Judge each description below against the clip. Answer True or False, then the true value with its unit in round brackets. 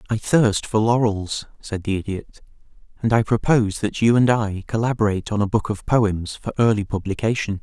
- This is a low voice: True (105 Hz)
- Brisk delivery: False (180 wpm)